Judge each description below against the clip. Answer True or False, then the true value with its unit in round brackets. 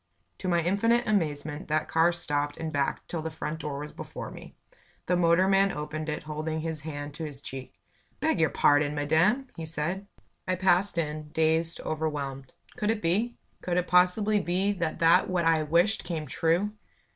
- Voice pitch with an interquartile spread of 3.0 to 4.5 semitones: True (3.3 semitones)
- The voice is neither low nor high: True (165 Hz)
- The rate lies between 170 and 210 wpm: True (180 wpm)